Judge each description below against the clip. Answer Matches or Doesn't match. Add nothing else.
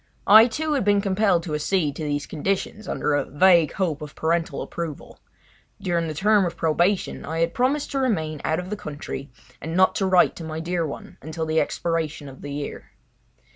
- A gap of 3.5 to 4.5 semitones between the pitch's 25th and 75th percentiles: Matches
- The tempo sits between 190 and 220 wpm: Matches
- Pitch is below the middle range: Doesn't match